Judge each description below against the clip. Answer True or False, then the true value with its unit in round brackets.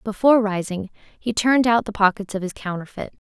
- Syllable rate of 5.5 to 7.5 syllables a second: True (5.8 syllables/s)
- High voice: True (210 Hz)